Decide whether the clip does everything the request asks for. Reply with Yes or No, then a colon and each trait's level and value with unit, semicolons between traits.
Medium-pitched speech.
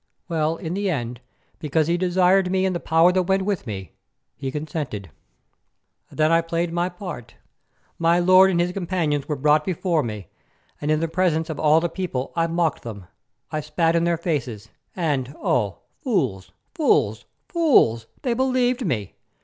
Yes: medium, 165 Hz